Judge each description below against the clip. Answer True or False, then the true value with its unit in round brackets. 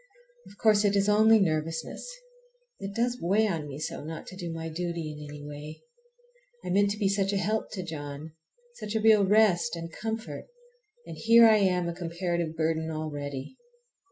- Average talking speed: True (185 wpm)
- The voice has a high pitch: False (175 Hz)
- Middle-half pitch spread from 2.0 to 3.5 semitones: False (4.7 semitones)